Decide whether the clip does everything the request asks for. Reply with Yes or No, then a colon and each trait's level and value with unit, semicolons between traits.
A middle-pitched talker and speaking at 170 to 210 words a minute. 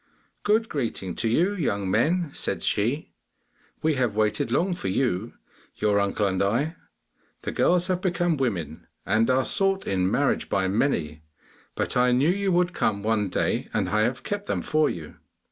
No: low, 125 Hz; average, 175 wpm